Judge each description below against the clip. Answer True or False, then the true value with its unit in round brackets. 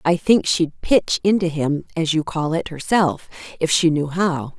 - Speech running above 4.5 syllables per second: False (4.2 syllables/s)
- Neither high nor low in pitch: True (165 Hz)